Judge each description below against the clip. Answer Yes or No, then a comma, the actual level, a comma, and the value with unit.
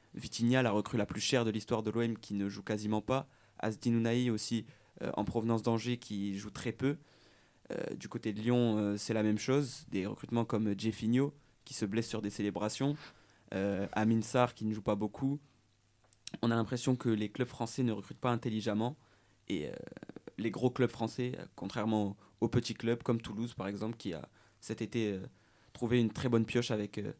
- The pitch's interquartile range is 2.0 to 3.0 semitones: Yes, narrow, 2.4 semitones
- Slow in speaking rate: No, average, 200 wpm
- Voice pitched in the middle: No, low, 115 Hz